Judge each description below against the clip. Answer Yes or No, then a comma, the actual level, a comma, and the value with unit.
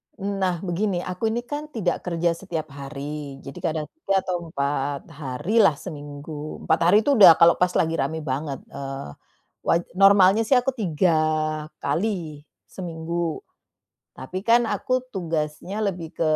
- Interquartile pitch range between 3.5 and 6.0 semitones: Yes, average, 4.5 semitones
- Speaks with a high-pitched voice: No, medium, 170 Hz